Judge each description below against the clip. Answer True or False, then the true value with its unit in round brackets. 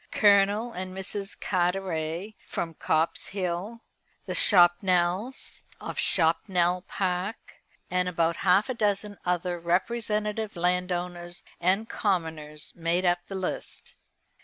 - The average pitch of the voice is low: False (180 Hz)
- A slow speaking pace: True (110 wpm)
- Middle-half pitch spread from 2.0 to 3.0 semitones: True (2.6 semitones)